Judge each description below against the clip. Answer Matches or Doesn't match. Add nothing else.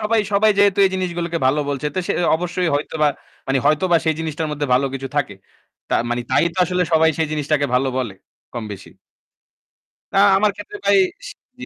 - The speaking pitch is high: Doesn't match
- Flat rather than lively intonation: Doesn't match